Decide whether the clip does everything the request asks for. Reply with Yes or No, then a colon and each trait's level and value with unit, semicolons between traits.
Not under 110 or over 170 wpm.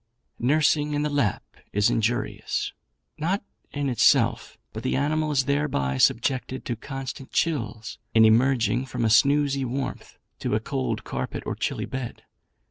Yes: average, 145 wpm